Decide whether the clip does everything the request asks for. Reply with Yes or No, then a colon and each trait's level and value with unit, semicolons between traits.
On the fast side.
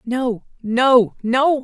No: slow, 110 wpm